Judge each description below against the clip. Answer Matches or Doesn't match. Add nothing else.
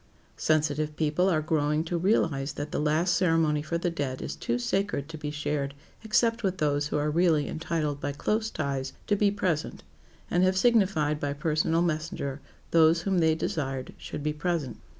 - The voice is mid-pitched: Matches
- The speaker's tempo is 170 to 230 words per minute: Matches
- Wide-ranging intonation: Doesn't match